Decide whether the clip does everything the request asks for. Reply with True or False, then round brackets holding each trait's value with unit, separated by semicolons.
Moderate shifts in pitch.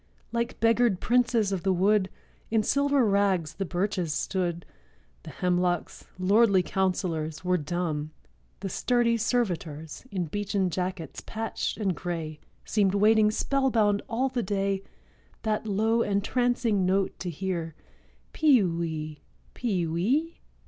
True (4.2 semitones)